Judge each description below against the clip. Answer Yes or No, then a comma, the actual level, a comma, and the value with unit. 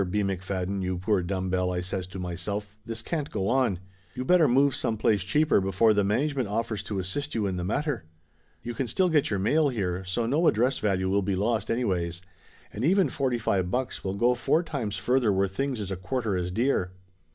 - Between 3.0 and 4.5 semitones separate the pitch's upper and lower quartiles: No, average, 5.2 semitones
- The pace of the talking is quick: Yes, fast, 215 wpm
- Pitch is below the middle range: Yes, low, 105 Hz